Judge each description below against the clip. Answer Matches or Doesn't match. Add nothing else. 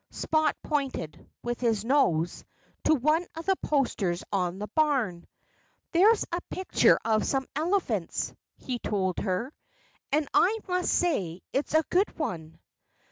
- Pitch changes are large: Matches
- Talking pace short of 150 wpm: Matches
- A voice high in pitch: Matches